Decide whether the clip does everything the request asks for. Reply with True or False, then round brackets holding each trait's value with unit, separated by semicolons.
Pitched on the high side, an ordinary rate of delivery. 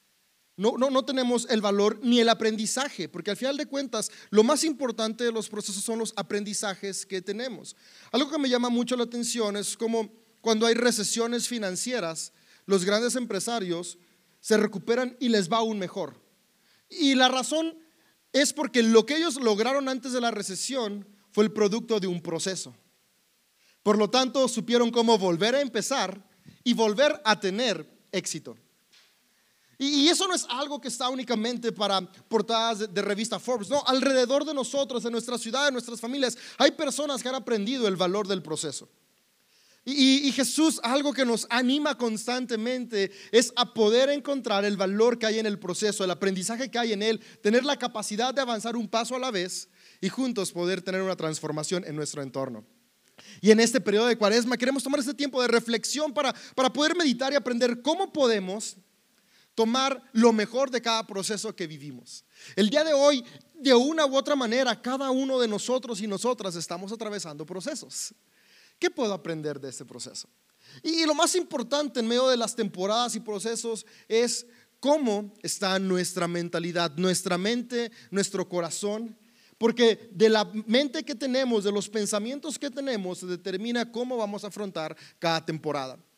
True (230 Hz; 175 wpm)